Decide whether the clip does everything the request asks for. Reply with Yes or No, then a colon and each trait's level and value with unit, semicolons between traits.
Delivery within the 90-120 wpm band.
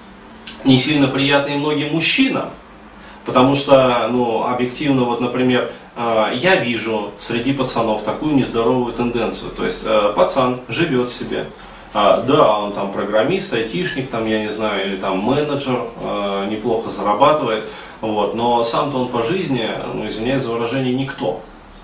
No: average, 130 wpm